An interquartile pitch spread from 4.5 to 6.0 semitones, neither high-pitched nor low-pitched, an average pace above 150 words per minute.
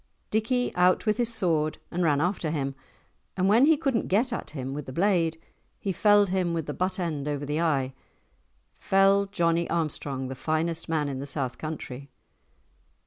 Yes: average, 5.0 semitones; medium, 165 Hz; average, 185 wpm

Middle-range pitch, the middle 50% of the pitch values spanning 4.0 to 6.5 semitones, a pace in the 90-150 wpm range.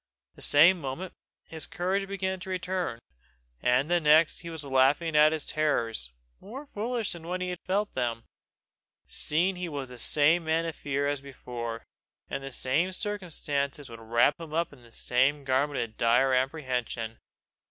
No: medium, 150 Hz; average, 5.2 semitones; average, 165 wpm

